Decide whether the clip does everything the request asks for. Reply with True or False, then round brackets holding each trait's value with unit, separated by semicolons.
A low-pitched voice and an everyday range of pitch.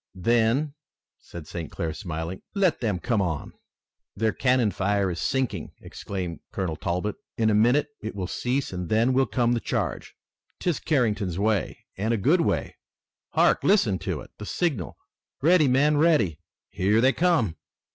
False (110 Hz; 6.1 semitones)